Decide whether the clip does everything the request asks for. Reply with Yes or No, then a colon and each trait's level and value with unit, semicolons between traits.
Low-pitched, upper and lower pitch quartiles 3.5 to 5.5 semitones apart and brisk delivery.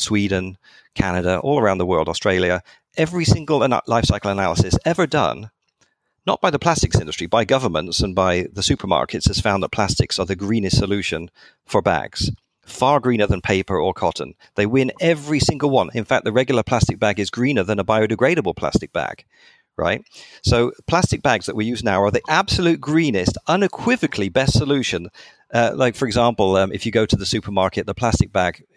No: low, 115 Hz; average, 4.9 semitones; average, 185 wpm